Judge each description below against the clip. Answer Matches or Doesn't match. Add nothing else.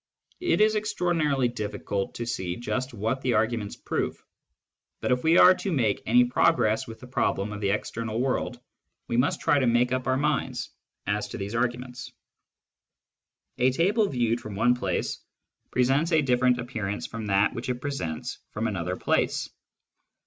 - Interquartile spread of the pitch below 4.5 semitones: Matches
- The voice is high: Doesn't match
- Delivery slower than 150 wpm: Doesn't match